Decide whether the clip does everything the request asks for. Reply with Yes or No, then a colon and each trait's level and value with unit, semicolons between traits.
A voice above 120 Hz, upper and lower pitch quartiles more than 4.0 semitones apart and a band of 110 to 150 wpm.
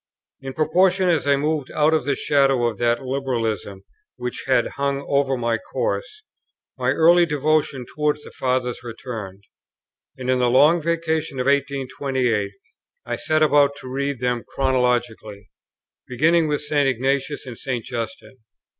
No: low, 135 Hz; average, 3.4 semitones; average, 145 wpm